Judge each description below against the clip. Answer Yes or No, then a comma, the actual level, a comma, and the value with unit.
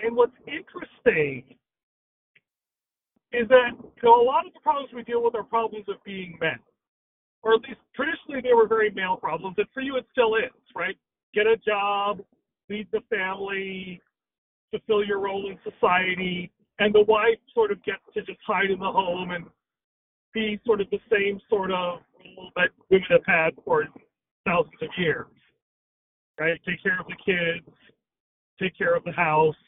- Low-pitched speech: No, high, 210 Hz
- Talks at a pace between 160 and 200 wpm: Yes, average, 175 wpm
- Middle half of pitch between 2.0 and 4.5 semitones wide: No, wide, 5.6 semitones